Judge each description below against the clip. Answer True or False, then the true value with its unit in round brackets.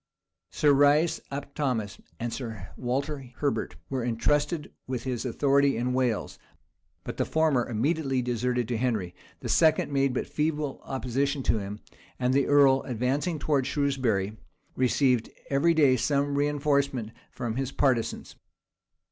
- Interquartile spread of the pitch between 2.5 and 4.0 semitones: True (2.8 semitones)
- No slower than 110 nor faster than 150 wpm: True (140 wpm)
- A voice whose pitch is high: False (135 Hz)